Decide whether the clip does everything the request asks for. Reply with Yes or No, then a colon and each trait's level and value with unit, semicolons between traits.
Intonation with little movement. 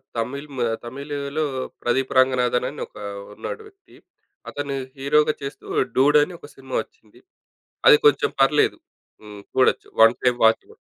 No: average, 3.0 semitones